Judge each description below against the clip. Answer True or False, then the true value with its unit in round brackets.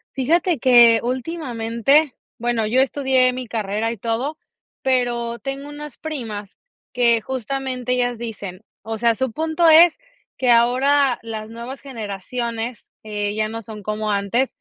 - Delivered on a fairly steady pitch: False (3.0 semitones)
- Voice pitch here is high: True (240 Hz)